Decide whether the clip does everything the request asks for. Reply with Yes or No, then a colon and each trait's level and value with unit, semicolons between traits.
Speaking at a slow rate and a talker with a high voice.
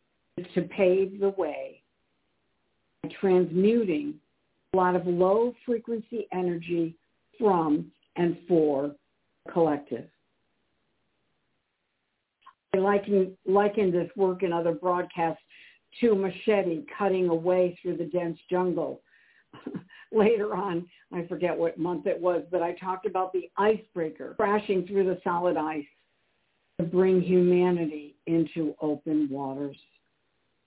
No: slow, 115 wpm; medium, 180 Hz